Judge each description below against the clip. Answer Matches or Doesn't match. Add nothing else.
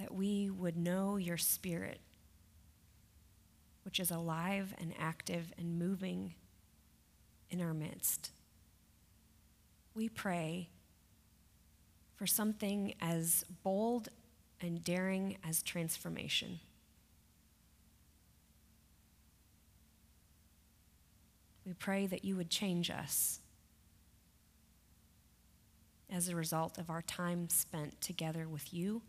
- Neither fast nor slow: Doesn't match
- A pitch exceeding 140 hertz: Doesn't match